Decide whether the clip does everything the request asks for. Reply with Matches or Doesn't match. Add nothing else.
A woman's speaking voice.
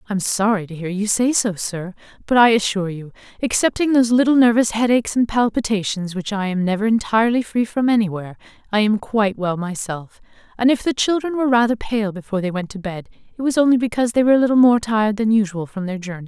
Matches